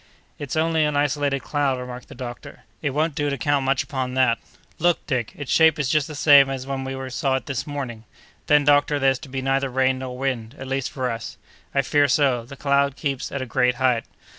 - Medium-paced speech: No, fast, 225 wpm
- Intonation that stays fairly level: Yes, narrow, 1.9 semitones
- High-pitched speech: No, low, 135 Hz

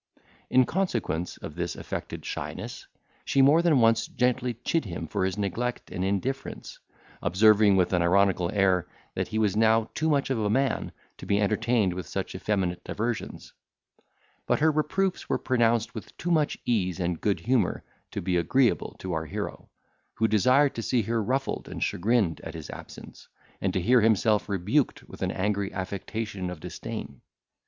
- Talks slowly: No, average, 170 wpm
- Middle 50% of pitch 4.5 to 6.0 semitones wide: Yes, average, 4.9 semitones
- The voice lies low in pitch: Yes, low, 110 Hz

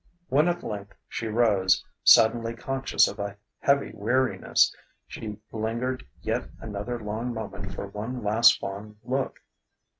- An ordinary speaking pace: No, slow, 130 wpm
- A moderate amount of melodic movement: Yes, average, 3.1 semitones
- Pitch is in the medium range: No, low, 110 Hz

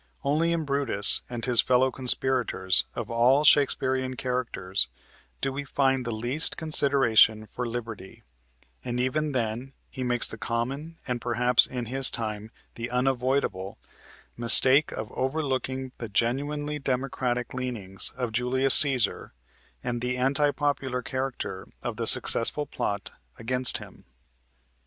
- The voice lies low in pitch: Yes, low, 125 Hz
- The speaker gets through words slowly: Yes, slow, 130 wpm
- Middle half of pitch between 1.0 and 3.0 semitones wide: Yes, narrow, 2.5 semitones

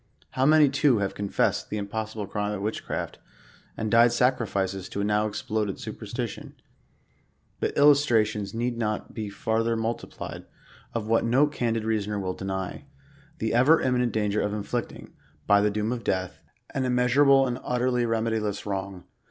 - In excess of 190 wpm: No, average, 170 wpm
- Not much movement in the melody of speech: No, average, 3.1 semitones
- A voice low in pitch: Yes, low, 110 Hz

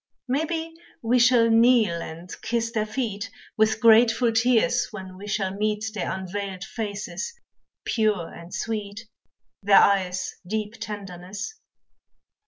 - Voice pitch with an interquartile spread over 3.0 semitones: No, average, 2.7 semitones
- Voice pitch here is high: Yes, high, 215 Hz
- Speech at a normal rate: No, slow, 120 wpm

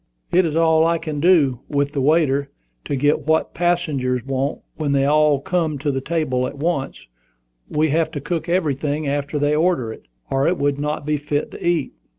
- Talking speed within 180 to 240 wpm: Yes, average, 200 wpm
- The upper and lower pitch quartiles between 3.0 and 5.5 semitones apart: No, narrow, 2.6 semitones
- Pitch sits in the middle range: Yes, medium, 150 Hz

